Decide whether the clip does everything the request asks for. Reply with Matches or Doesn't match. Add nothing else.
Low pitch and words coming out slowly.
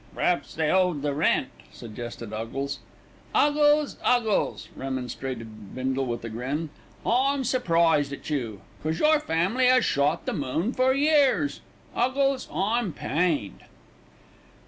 Doesn't match